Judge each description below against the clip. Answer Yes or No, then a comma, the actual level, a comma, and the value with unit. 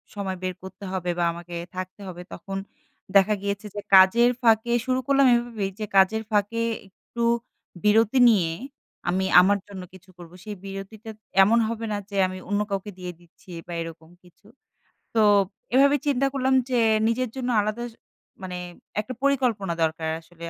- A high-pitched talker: Yes, high, 205 Hz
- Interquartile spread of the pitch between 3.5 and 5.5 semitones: Yes, average, 3.8 semitones